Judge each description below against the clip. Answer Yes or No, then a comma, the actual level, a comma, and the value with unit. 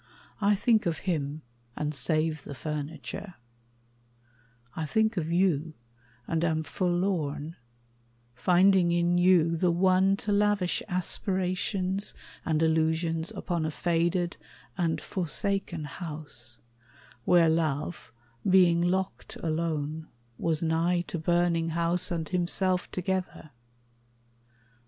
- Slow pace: Yes, slow, 105 wpm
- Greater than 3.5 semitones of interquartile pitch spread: No, narrow, 2.5 semitones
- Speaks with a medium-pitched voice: Yes, medium, 170 Hz